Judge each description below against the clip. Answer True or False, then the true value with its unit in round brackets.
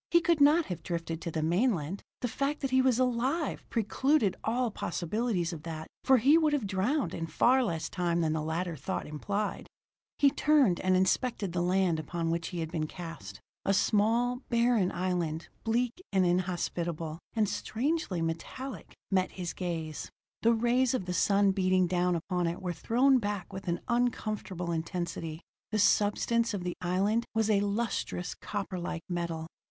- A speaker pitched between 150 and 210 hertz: True (190 Hz)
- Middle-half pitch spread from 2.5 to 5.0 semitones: False (5.6 semitones)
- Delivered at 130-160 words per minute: False (170 wpm)